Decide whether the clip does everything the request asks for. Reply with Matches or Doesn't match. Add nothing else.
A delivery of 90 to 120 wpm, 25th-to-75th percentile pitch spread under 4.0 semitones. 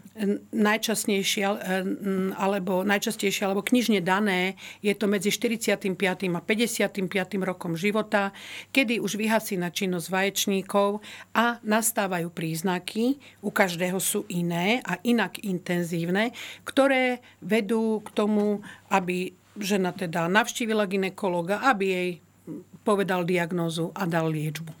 Matches